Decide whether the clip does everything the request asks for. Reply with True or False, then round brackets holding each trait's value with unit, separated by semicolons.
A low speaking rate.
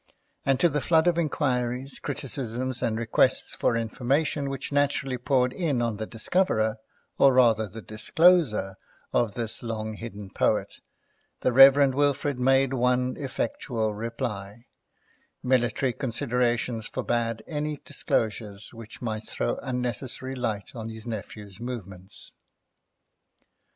True (120 wpm)